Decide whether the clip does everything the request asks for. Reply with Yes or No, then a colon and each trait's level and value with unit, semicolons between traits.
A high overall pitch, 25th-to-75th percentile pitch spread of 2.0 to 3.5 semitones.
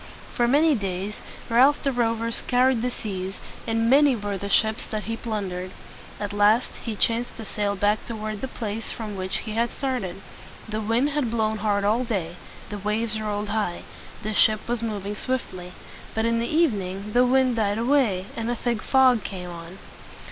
Yes: high, 220 Hz; average, 2.8 semitones